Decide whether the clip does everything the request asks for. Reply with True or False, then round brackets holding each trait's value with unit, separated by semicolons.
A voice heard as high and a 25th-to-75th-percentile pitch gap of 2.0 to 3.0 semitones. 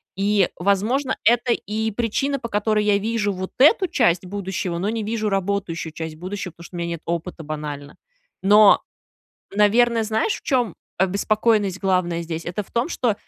False (200 Hz; 4.0 semitones)